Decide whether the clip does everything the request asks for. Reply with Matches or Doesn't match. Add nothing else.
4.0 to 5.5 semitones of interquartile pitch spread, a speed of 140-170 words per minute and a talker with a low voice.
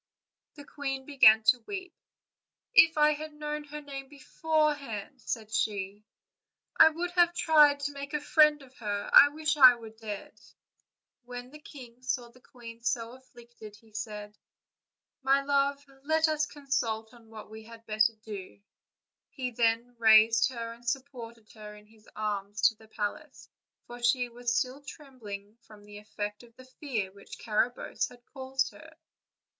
Doesn't match